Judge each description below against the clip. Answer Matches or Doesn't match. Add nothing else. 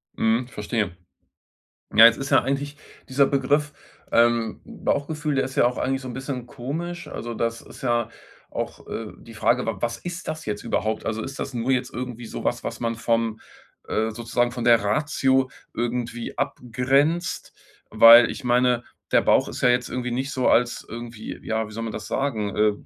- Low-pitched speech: Matches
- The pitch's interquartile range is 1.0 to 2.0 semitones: Doesn't match